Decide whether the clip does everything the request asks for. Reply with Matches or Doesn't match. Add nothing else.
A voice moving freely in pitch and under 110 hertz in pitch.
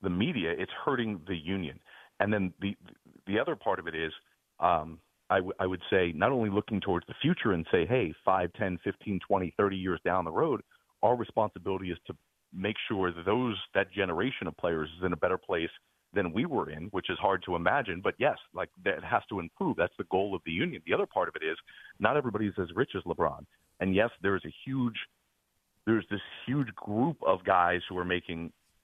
Doesn't match